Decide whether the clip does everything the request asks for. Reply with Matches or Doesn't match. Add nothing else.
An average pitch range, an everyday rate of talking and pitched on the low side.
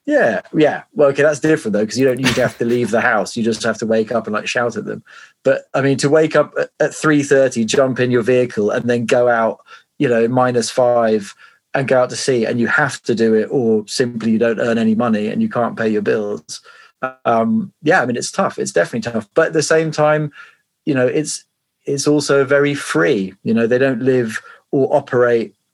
Doesn't match